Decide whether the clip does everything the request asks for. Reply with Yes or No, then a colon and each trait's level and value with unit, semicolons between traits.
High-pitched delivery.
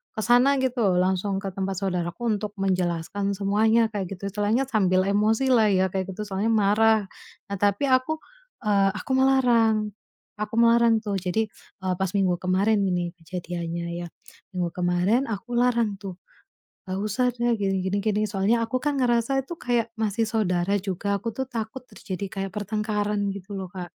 Yes: high, 205 Hz